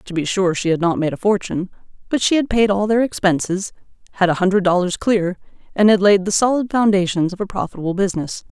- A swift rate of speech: Yes, fast, 215 wpm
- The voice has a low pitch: No, high, 190 Hz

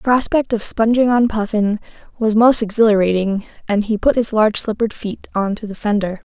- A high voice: Yes, high, 215 Hz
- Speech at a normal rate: Yes, average, 190 wpm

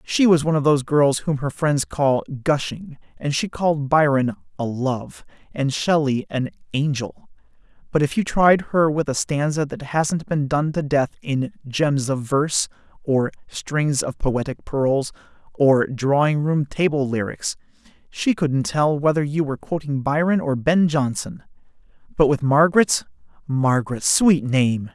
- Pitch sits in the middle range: Yes, medium, 145 Hz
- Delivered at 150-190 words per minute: Yes, average, 155 wpm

